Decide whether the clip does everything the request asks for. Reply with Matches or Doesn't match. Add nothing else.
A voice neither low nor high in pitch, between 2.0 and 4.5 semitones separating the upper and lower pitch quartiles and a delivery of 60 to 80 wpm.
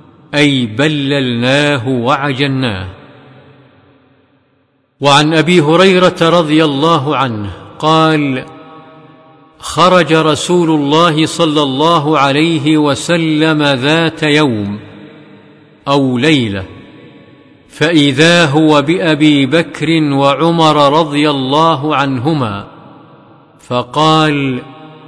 Matches